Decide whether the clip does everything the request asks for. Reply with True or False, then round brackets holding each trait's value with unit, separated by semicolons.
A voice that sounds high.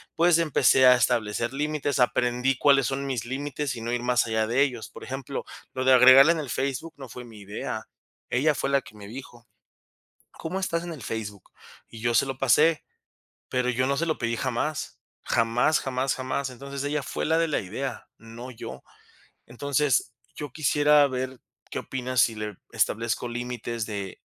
False (130 Hz)